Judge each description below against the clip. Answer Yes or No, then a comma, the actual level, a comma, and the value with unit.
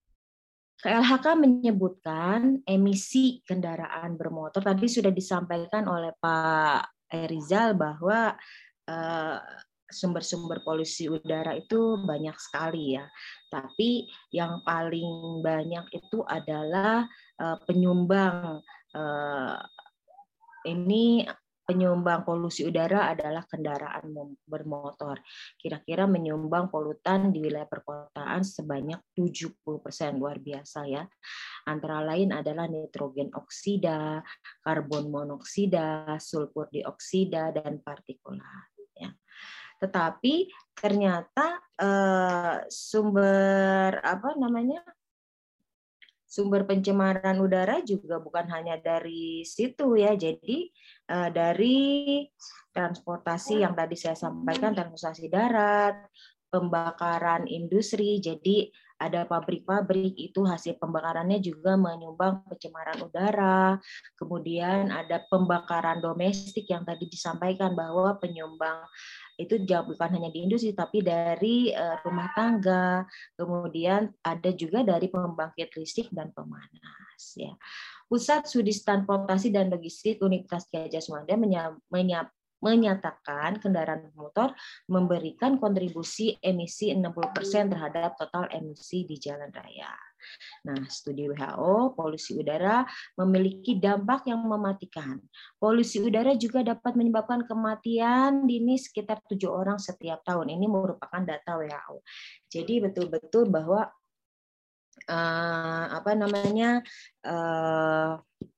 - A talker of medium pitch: Yes, medium, 180 Hz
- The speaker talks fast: No, average, 95 wpm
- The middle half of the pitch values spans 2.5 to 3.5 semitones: No, average, 4.2 semitones